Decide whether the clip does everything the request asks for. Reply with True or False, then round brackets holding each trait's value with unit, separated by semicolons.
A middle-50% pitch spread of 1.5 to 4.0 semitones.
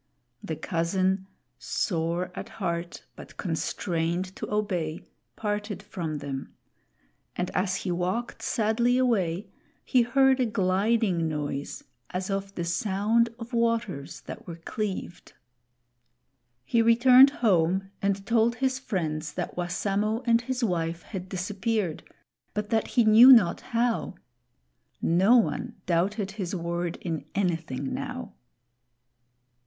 False (5.0 semitones)